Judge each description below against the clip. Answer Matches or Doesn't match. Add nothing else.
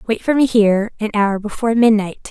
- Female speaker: Matches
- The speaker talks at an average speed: Doesn't match